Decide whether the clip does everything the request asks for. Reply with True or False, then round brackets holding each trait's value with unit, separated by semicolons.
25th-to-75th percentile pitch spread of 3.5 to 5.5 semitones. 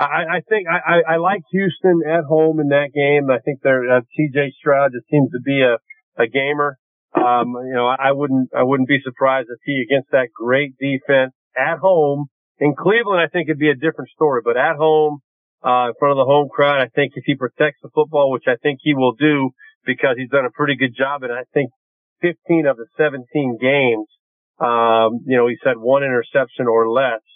False (2.8 semitones)